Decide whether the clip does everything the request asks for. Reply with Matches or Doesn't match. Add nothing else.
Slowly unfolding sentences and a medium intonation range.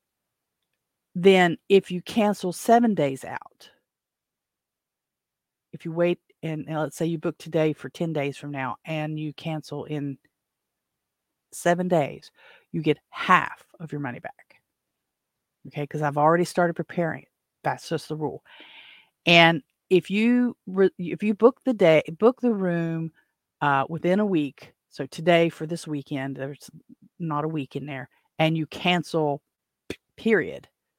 Doesn't match